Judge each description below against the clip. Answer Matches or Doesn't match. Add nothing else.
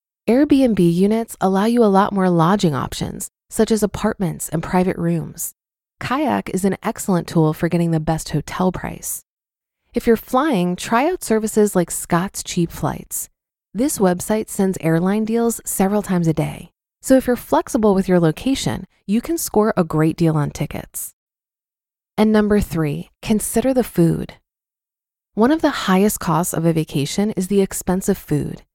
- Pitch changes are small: Doesn't match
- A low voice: Doesn't match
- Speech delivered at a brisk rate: Doesn't match